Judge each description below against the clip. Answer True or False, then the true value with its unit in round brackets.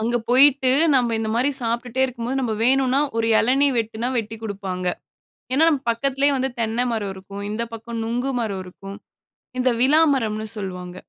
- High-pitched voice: True (235 Hz)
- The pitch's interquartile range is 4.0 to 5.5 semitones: False (3.3 semitones)